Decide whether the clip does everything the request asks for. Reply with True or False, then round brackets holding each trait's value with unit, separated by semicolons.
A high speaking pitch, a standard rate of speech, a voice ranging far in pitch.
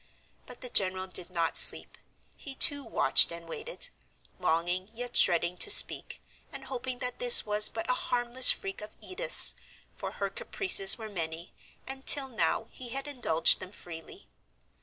True (225 Hz; 160 wpm; 6.5 semitones)